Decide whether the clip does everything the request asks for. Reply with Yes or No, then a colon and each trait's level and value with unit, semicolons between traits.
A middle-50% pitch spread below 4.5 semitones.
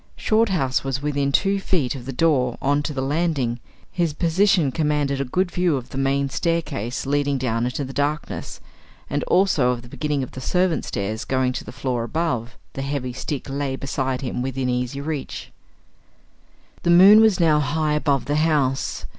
Yes: average, 3.7 semitones